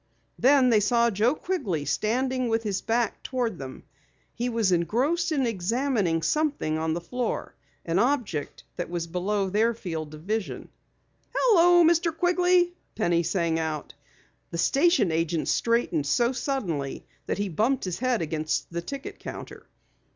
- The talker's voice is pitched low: No, high, 220 Hz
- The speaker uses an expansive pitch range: Yes, wide, 7.6 semitones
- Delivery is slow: No, average, 150 wpm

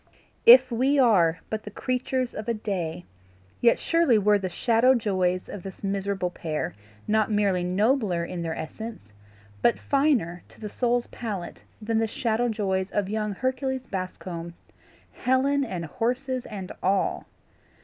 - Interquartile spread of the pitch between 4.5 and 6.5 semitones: Yes, average, 4.9 semitones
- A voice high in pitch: Yes, high, 210 Hz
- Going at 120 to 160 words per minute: Yes, average, 150 wpm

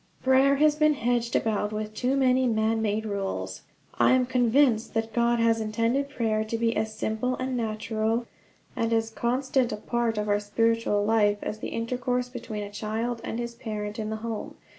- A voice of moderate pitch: No, high, 230 Hz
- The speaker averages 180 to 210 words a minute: Yes, average, 185 wpm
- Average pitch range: No, narrow, 2.3 semitones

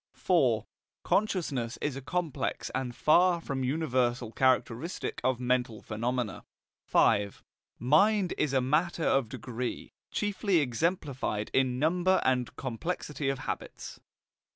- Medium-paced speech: No, slow, 115 wpm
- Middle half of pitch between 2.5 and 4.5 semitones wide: No, average, 5.0 semitones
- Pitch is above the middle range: No, low, 130 Hz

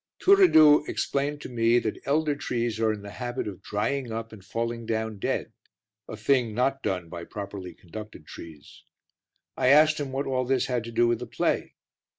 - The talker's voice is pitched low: Yes, low, 115 Hz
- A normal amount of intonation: Yes, average, 4.2 semitones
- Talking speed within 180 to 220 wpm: Yes, average, 185 wpm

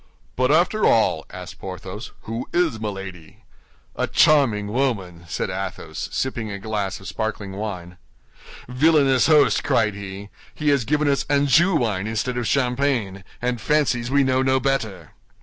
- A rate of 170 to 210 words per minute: No, average, 150 wpm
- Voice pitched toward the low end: Yes, low, 120 Hz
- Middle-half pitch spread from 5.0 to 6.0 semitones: Yes, wide, 5.6 semitones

